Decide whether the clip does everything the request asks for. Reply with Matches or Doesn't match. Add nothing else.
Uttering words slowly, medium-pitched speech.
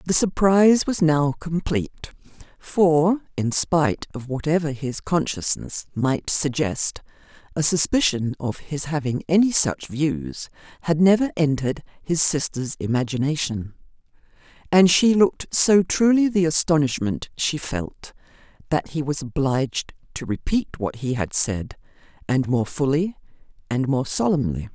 Matches